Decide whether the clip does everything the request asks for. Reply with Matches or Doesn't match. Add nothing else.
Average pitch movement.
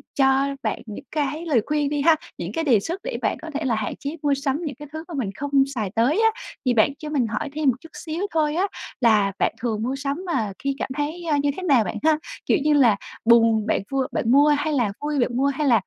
Matches